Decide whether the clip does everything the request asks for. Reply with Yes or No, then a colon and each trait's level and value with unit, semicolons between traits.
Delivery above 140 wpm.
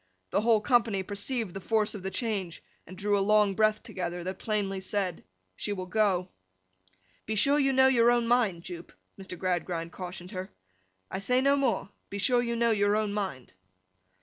Yes: average, 185 wpm